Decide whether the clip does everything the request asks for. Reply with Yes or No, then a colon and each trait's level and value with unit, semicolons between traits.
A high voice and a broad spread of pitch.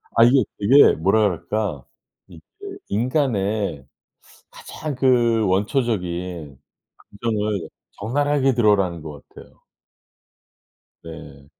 No: low, 105 Hz; wide, 5.8 semitones